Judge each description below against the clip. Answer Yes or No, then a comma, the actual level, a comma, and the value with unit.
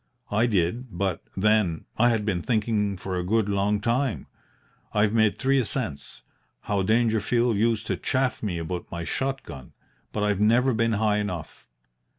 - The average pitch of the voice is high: No, low, 105 Hz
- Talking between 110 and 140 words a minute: No, average, 160 wpm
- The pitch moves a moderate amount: Yes, average, 3.2 semitones